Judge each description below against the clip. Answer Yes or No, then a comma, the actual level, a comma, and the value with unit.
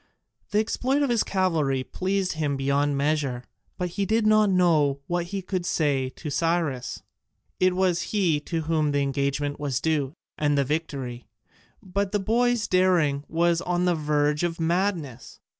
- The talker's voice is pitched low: No, medium, 165 Hz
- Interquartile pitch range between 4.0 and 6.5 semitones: Yes, average, 4.5 semitones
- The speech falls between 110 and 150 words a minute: No, average, 160 wpm